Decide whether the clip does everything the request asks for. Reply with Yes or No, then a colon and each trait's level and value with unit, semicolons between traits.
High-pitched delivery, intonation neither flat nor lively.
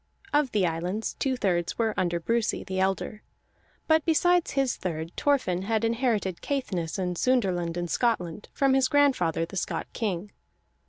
No: high, 210 Hz; wide, 6.6 semitones